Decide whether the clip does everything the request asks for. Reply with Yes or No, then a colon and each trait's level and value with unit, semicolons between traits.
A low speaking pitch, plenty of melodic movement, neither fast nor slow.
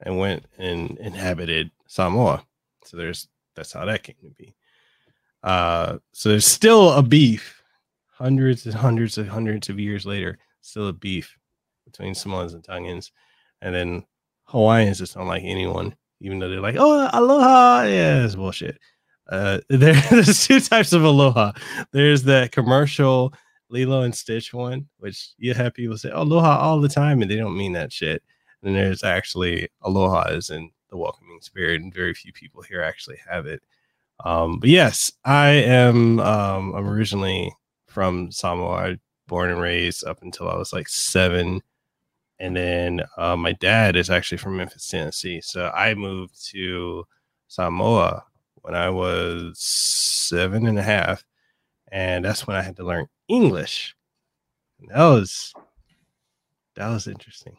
Yes: low, 100 Hz; wide, 5.7 semitones; average, 160 wpm